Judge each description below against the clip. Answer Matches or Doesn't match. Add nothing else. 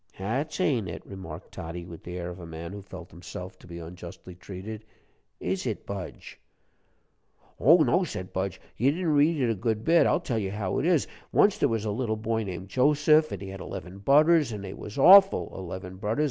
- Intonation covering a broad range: Matches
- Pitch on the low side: Matches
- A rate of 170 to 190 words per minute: Doesn't match